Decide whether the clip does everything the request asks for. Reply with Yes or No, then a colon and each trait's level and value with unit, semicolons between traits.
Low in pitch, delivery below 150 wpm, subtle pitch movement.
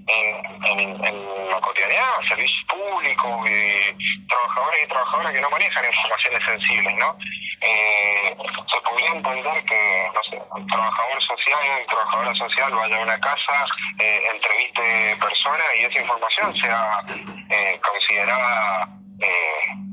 Yes: low, 110 Hz; average, 130 wpm; narrow, 1.7 semitones